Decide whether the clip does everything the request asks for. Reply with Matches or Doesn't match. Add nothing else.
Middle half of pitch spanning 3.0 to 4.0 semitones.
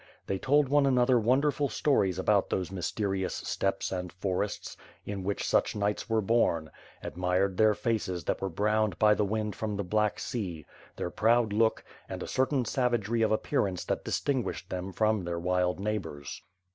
Matches